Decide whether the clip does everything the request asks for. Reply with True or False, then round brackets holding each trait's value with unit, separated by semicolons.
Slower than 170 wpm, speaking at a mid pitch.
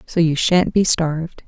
False (205 wpm; 165 Hz)